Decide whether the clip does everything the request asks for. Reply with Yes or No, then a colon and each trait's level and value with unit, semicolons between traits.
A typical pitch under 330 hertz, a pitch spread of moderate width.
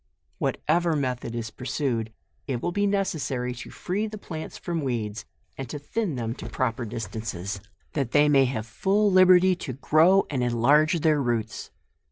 No: low, 135 Hz; wide, 6.4 semitones